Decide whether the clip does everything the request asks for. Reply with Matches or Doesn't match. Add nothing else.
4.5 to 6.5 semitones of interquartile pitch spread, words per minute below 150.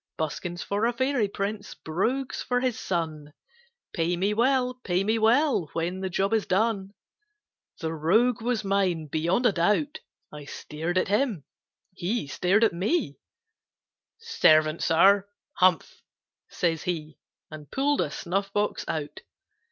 Matches